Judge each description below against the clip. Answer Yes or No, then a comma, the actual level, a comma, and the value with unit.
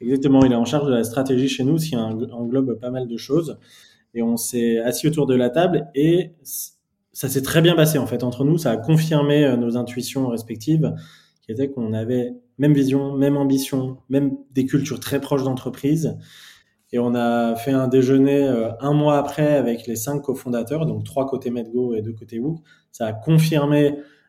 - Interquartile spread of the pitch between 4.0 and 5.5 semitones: No, average, 3.1 semitones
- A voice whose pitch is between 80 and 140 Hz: Yes, low, 135 Hz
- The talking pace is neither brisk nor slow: Yes, average, 195 wpm